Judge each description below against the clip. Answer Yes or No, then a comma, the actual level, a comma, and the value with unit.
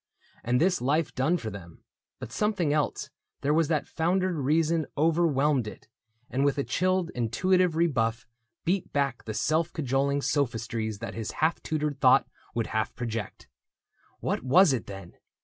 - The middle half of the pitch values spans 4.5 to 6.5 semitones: Yes, wide, 5.6 semitones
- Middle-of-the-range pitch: Yes, medium, 145 Hz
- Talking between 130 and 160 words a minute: Yes, average, 155 wpm